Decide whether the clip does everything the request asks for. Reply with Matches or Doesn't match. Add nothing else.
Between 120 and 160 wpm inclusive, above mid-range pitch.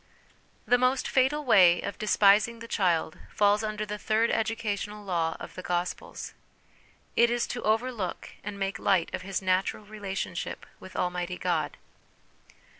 Matches